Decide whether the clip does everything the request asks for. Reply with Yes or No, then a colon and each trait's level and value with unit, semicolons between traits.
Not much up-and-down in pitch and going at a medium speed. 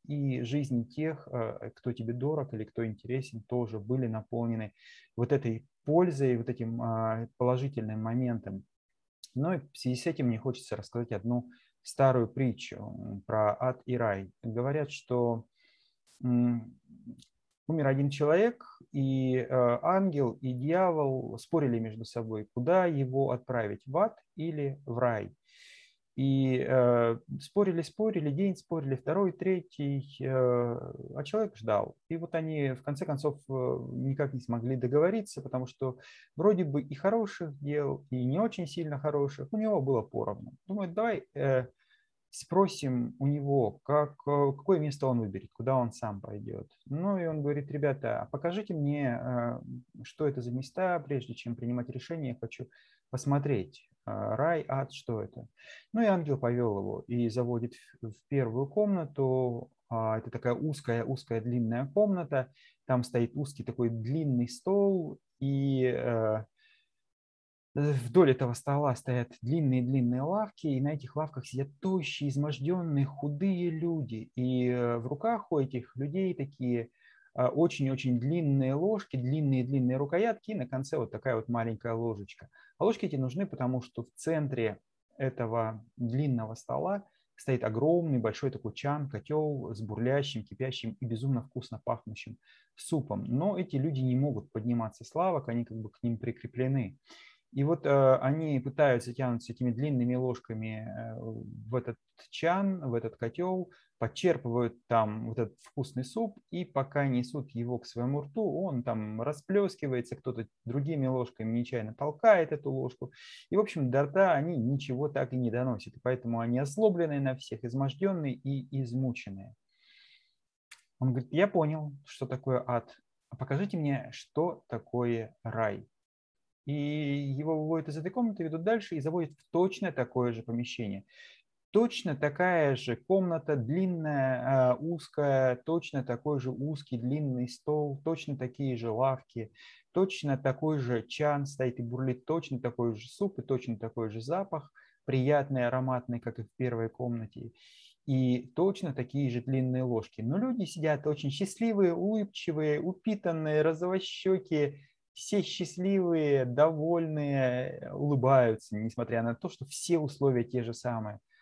No: average, 4.3 semitones; average, 140 wpm